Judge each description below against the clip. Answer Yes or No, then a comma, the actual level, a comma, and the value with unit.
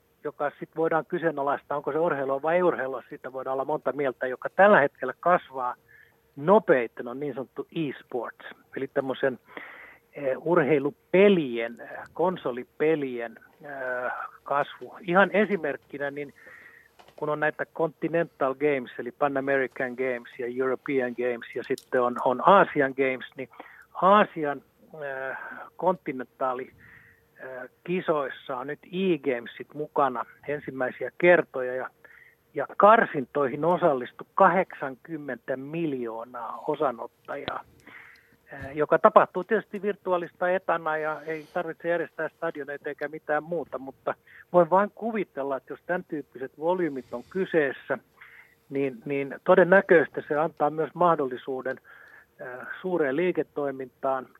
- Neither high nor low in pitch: Yes, medium, 145 Hz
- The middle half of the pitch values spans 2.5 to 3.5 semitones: No, average, 4.4 semitones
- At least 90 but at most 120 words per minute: Yes, average, 110 wpm